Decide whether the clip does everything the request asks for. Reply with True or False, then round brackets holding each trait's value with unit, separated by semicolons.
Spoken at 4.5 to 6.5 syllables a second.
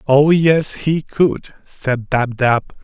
False (2.9 syllables/s)